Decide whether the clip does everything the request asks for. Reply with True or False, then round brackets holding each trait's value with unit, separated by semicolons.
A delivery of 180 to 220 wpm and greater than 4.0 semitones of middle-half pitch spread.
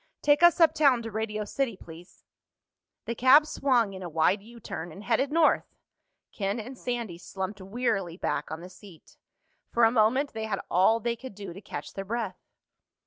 True (185 wpm; 4.4 semitones)